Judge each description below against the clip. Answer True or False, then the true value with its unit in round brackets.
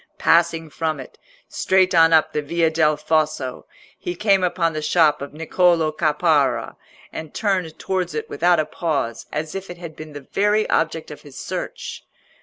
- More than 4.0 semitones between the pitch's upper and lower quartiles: False (2.6 semitones)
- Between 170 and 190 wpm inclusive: True (175 wpm)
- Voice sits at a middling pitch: True (160 Hz)